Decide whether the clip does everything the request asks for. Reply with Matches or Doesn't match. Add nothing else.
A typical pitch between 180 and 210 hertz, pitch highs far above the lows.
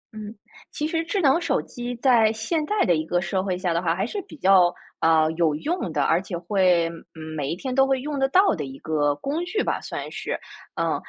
Matches